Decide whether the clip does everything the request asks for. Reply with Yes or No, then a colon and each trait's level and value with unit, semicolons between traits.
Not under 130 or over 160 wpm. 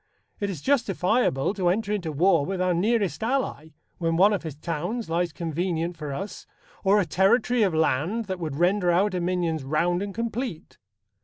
No: average, 175 wpm